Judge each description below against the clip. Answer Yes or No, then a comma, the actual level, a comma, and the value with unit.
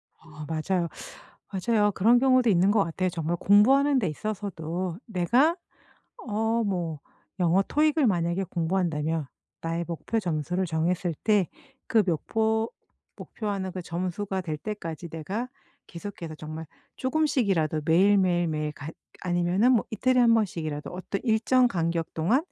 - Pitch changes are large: No, average, 4.8 semitones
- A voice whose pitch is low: No, medium, 185 Hz